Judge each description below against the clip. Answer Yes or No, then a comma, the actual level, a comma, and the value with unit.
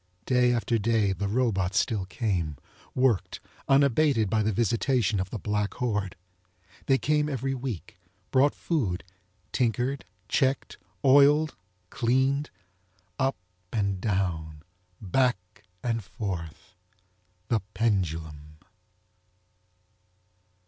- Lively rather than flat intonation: Yes, wide, 5.8 semitones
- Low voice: Yes, low, 110 Hz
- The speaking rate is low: Yes, slow, 95 wpm